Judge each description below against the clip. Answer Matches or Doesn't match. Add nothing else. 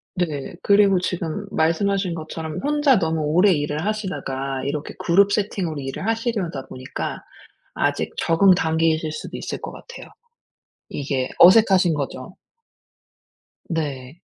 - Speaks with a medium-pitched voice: Matches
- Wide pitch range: Doesn't match